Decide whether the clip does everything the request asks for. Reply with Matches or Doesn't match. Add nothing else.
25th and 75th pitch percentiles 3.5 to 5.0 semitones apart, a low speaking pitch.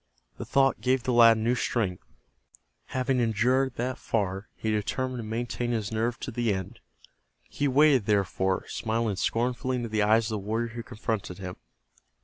Doesn't match